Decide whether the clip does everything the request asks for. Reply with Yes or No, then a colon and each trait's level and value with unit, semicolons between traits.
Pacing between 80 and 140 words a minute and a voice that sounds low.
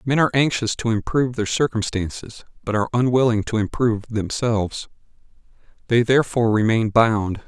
Yes: slow, 135 wpm; low, 115 Hz